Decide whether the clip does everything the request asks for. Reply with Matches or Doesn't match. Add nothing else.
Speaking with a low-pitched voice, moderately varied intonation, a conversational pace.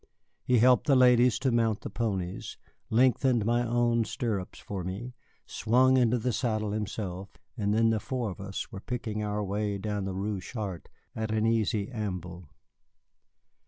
Matches